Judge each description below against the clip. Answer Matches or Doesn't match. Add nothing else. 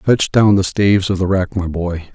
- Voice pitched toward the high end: Doesn't match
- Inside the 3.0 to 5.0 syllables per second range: Matches